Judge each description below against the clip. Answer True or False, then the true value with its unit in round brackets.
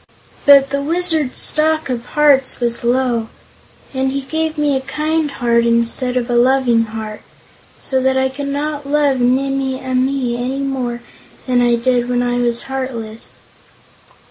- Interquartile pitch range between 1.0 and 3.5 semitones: True (2.5 semitones)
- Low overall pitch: False (260 Hz)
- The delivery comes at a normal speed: True (155 wpm)